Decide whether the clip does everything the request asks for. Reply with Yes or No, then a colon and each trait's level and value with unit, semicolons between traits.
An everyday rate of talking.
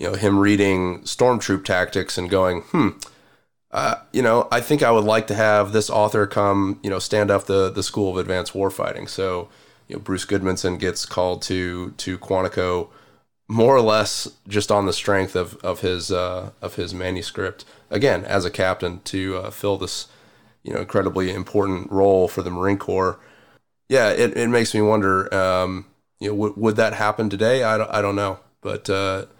Yes: average, 190 wpm